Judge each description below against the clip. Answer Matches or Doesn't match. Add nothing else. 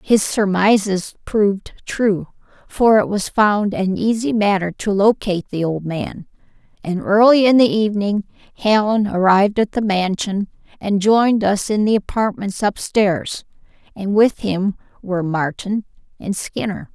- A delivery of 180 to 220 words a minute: Doesn't match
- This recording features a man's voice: Doesn't match